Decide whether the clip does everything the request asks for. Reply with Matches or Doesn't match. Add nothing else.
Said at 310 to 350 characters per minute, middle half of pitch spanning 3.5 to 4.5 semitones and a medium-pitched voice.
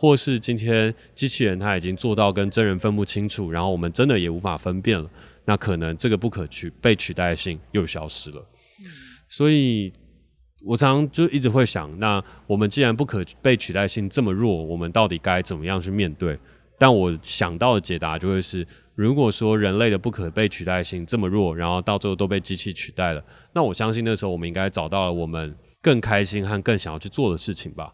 Doesn't match